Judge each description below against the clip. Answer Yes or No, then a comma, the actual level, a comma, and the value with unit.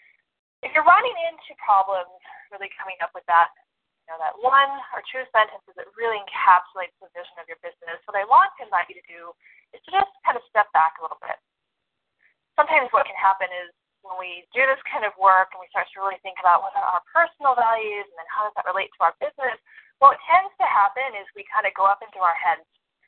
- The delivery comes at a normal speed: No, fast, 235 wpm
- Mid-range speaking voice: No, high, 200 Hz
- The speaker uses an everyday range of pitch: No, wide, 6.7 semitones